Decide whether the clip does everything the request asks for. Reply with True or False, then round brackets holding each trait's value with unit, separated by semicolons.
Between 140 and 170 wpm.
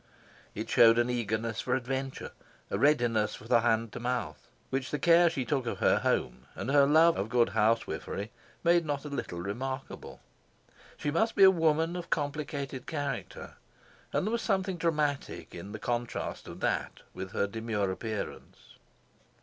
True (165 wpm)